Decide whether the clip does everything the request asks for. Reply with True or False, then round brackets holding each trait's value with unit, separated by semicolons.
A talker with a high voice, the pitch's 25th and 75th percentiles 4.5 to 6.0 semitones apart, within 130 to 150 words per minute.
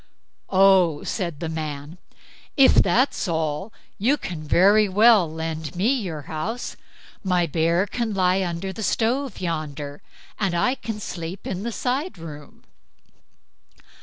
False (180 Hz; 5.0 semitones; 135 wpm)